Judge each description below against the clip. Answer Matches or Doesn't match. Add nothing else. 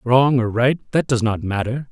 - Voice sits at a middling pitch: Doesn't match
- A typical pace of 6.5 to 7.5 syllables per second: Doesn't match